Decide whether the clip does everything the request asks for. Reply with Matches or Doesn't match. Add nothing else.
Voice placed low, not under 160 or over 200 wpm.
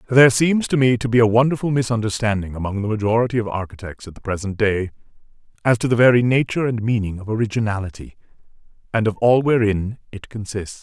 Matches